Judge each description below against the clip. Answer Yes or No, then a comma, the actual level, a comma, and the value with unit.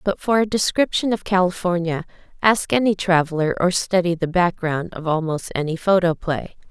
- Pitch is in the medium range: Yes, medium, 180 Hz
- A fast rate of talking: No, average, 150 wpm